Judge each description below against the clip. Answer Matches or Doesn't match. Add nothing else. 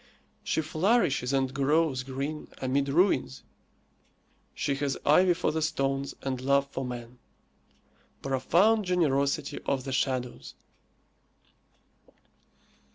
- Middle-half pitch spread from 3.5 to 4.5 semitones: Doesn't match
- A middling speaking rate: Doesn't match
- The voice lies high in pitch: Doesn't match